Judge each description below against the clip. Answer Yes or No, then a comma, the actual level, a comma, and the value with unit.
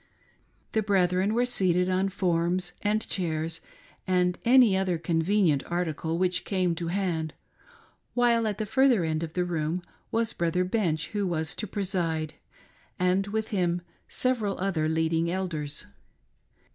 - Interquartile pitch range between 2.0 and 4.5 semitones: Yes, average, 3.4 semitones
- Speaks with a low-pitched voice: No, medium, 180 Hz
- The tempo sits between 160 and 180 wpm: No, average, 140 wpm